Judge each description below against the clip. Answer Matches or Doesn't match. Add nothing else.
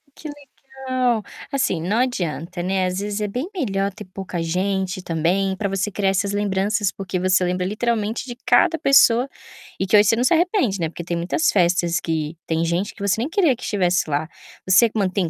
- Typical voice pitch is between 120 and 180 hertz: Doesn't match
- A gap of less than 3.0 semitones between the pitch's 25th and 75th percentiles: Doesn't match